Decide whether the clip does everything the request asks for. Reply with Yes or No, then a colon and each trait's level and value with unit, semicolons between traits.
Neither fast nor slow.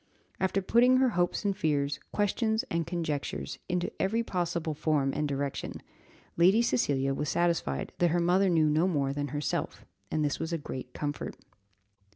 Yes: average, 165 wpm